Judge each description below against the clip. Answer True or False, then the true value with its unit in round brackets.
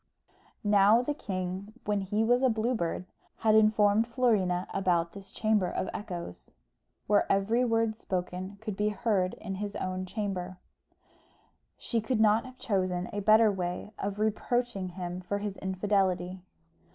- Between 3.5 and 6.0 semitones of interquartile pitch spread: False (2.9 semitones)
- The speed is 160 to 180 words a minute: False (150 wpm)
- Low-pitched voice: False (205 Hz)